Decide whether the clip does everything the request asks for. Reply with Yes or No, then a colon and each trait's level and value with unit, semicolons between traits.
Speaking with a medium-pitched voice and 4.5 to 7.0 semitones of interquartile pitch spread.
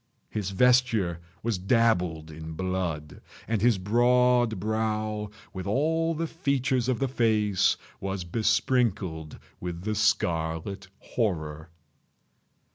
No: low, 105 Hz; average, 5.2 semitones